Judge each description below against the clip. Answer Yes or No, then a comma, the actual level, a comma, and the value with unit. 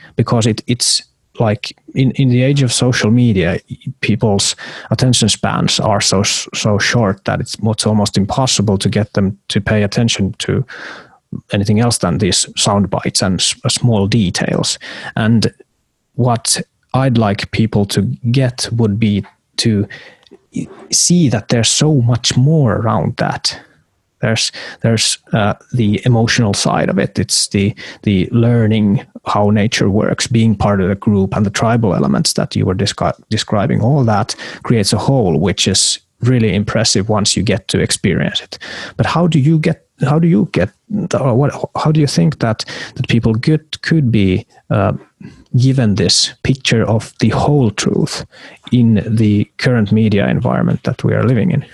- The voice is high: No, low, 115 Hz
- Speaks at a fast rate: Yes, fast, 160 wpm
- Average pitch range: Yes, average, 3.5 semitones